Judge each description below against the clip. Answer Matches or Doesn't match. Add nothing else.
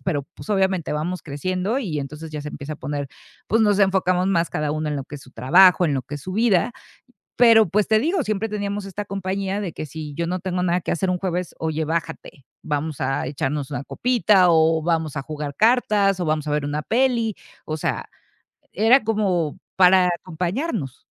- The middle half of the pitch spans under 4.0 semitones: Doesn't match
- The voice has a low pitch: Doesn't match